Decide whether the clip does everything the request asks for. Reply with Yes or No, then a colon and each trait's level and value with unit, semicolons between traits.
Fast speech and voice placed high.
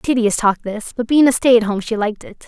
Yes: fast, 290 wpm; high, 230 Hz